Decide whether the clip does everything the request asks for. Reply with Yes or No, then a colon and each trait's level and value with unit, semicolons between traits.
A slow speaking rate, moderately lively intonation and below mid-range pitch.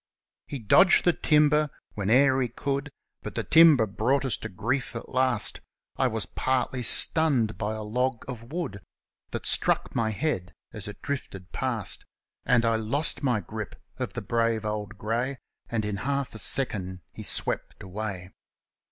No: average, 155 wpm; average, 4.6 semitones; low, 115 Hz